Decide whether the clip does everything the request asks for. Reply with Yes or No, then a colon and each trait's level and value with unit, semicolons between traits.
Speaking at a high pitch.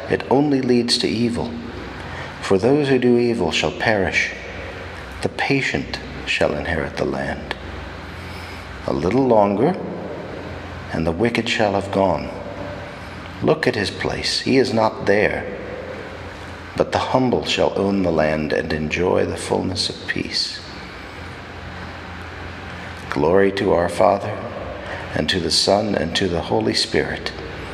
No: very low, 95 Hz